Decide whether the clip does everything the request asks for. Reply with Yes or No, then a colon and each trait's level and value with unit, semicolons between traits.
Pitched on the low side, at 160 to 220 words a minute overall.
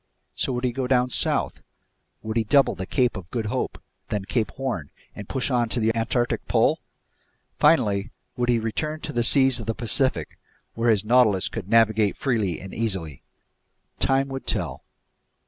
Yes: low, 115 Hz; average, 175 wpm